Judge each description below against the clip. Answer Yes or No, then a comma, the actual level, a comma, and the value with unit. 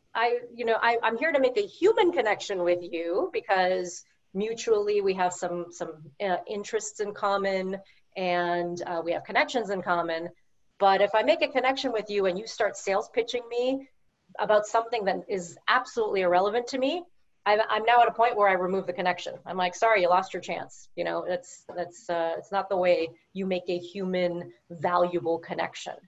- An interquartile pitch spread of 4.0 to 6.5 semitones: Yes, average, 4.3 semitones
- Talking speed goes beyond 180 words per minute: Yes, average, 195 wpm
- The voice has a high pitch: Yes, high, 195 Hz